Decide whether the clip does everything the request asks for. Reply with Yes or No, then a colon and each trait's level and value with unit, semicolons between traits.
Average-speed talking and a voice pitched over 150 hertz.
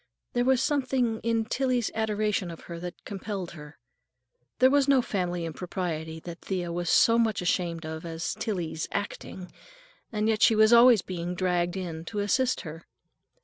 Yes: average, 165 wpm; high, 190 Hz